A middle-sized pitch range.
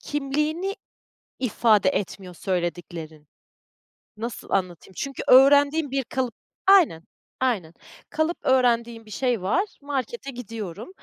No: wide, 6.7 semitones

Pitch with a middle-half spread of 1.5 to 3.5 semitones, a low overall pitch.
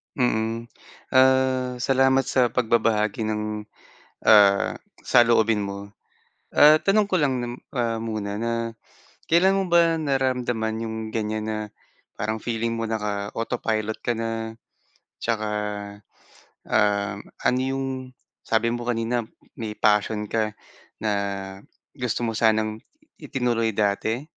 Yes: average, 2.7 semitones; low, 115 Hz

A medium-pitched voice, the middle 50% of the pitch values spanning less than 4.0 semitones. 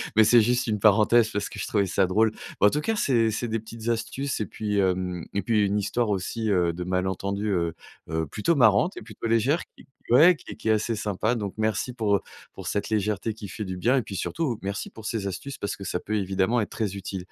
No: low, 105 Hz; average, 2.8 semitones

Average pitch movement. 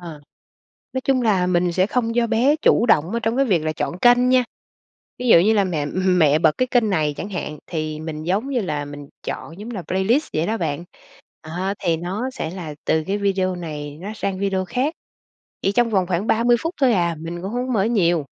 No: wide, 5.8 semitones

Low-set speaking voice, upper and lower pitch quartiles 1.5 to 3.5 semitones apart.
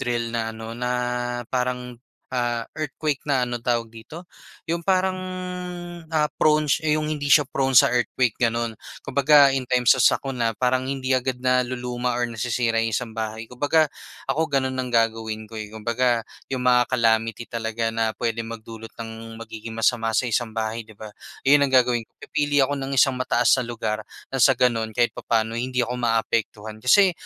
Yes: low, 120 Hz; narrow, 2.6 semitones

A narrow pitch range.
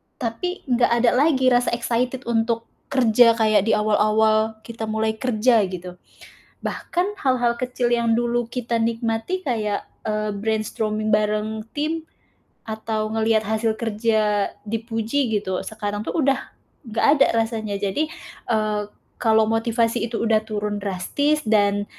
Yes: narrow, 2.0 semitones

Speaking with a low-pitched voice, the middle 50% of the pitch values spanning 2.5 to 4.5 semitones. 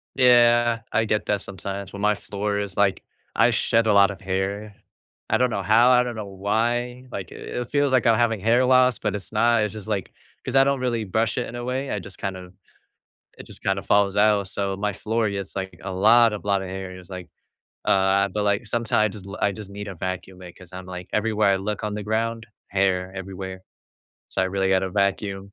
Yes: low, 105 Hz; average, 2.9 semitones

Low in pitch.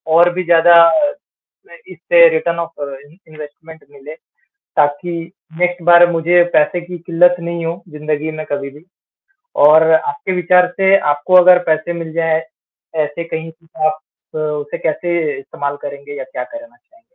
No: medium, 165 Hz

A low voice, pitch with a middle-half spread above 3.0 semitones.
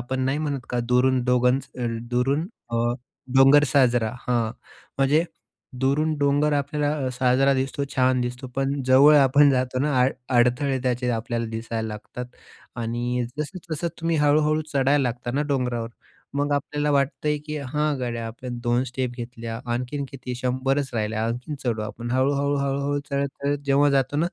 No: low, 130 Hz; average, 2.7 semitones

